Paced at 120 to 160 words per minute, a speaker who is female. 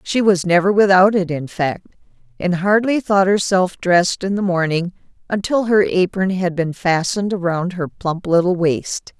No: average, 170 wpm; female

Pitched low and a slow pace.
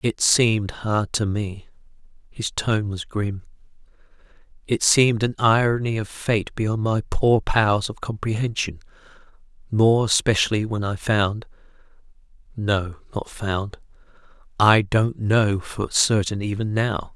Yes: low, 105 Hz; slow, 120 wpm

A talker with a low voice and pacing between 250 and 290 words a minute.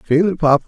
No: medium, 160 Hz; fast, 270 wpm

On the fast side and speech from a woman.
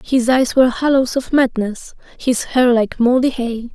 No: average, 175 wpm; female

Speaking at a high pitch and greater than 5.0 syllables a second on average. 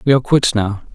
No: low, 120 Hz; 6.7 syllables/s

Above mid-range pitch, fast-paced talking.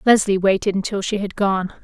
No: high, 200 Hz; average, 195 wpm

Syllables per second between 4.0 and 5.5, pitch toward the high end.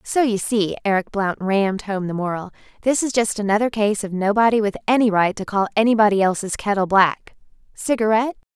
No: 5.8 syllables/s; high, 210 Hz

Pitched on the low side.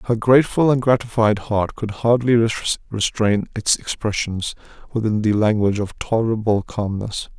Yes: low, 110 Hz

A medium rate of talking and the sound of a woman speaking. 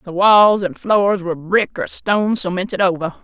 Yes: average, 185 wpm; female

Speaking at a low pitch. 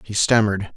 Yes: low, 105 Hz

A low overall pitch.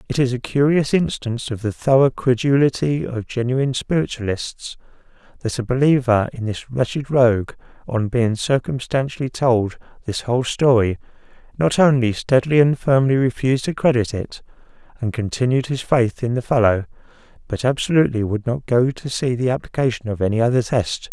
Yes: low, 125 Hz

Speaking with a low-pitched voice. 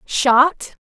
No: very high, 275 Hz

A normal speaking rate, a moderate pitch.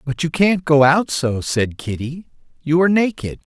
Yes: average, 185 wpm; medium, 155 Hz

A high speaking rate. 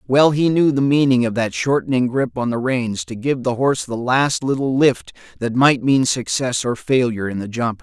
Yes: fast, 220 wpm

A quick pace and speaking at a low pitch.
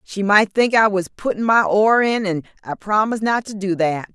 No: fast, 230 wpm; high, 205 Hz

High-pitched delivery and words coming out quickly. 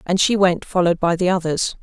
No: medium, 180 Hz; fast, 230 wpm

